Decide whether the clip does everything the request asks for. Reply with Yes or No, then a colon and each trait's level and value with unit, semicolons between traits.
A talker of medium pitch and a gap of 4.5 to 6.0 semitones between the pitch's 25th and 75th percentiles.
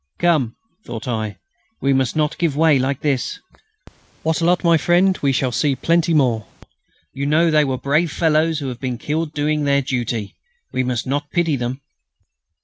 No: medium, 145 Hz; average, 3.8 semitones